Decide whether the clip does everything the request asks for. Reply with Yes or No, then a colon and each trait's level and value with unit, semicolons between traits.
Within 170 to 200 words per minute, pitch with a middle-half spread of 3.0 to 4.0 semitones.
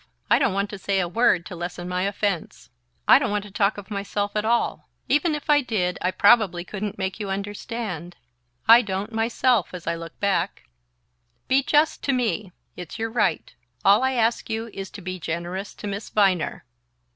Yes: average, 190 wpm; average, 3.6 semitones